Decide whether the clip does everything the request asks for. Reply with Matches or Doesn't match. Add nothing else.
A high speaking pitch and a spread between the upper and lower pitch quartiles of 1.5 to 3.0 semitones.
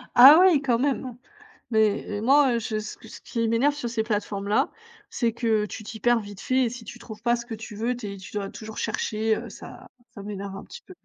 Matches